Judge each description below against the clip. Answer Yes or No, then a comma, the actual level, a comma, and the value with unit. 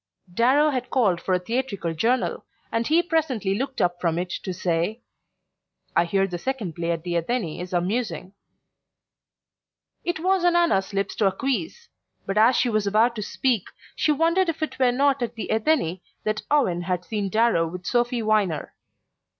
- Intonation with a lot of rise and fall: Yes, wide, 6.5 semitones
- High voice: Yes, high, 220 Hz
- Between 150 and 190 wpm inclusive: Yes, average, 175 wpm